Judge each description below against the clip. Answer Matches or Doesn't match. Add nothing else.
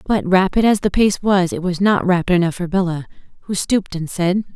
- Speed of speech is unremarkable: Doesn't match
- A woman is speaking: Matches